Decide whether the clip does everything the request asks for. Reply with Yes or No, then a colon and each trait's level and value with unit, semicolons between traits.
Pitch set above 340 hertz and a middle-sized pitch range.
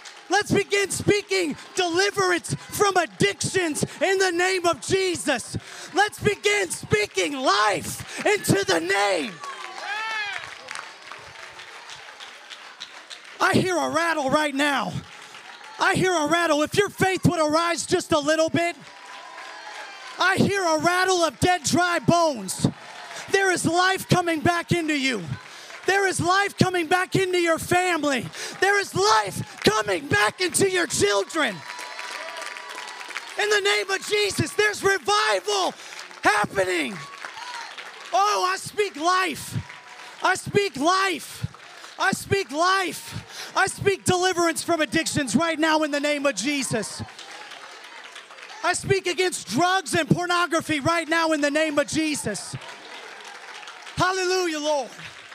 Yes: very high, 355 Hz; average, 3.7 semitones